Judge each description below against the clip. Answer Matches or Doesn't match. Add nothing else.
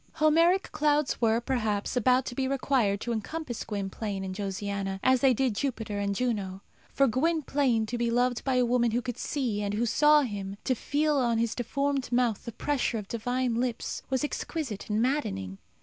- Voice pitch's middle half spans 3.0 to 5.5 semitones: Matches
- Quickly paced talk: Doesn't match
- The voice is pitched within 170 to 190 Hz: Doesn't match